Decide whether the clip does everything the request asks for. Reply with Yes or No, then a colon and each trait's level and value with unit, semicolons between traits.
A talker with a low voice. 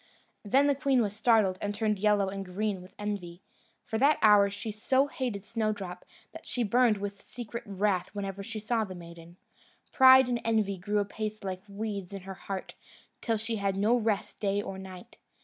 No: high, 205 Hz